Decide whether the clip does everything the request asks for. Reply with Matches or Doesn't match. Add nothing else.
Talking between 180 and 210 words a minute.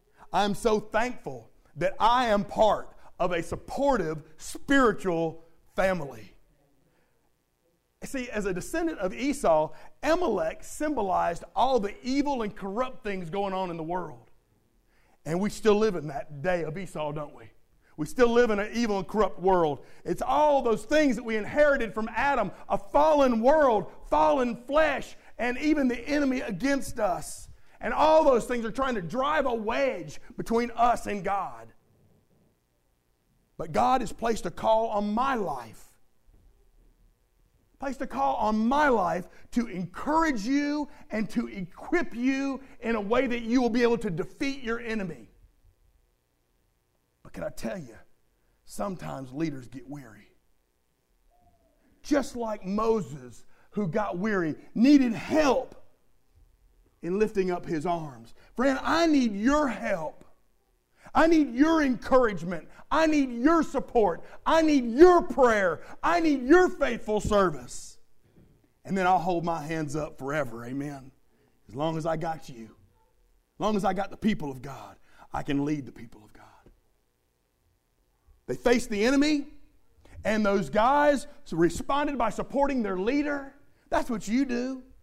Doesn't match